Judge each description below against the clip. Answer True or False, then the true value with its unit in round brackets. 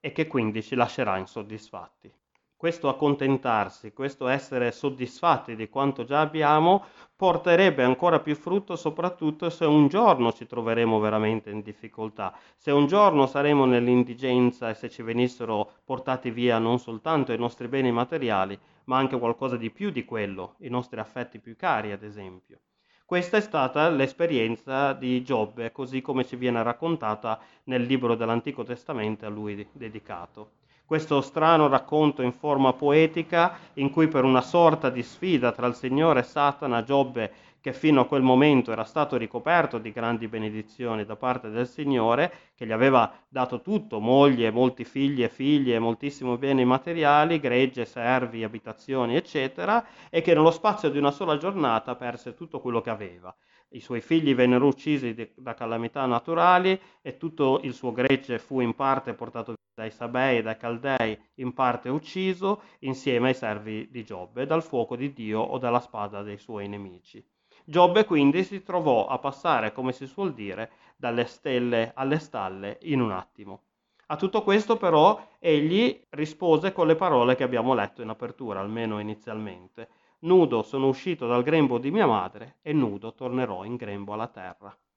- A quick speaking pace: False (160 wpm)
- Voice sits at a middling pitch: False (125 Hz)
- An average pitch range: True (4.5 semitones)